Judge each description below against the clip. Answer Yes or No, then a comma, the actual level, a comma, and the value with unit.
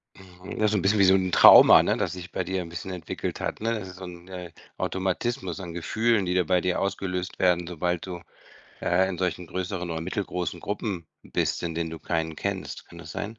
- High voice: No, very low, 90 Hz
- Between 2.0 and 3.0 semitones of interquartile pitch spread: No, narrow, 1.6 semitones